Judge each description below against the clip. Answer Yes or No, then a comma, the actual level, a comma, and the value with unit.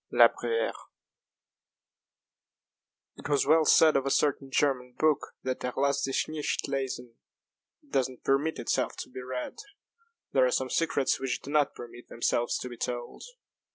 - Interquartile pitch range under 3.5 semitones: Yes, narrow, 2.6 semitones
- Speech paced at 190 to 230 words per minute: No, average, 160 wpm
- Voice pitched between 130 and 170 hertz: Yes, low, 135 Hz